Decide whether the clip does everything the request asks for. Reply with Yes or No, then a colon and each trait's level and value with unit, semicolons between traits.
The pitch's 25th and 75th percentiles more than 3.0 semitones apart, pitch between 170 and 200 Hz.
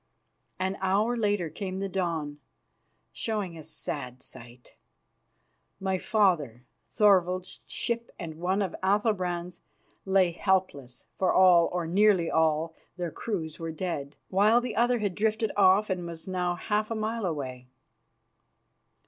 Yes: average, 3.9 semitones; medium, 185 Hz